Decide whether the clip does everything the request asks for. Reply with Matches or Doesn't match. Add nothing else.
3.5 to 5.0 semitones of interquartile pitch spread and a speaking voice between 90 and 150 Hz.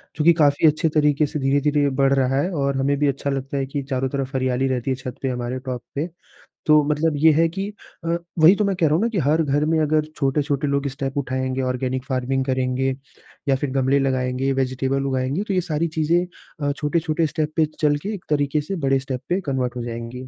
Doesn't match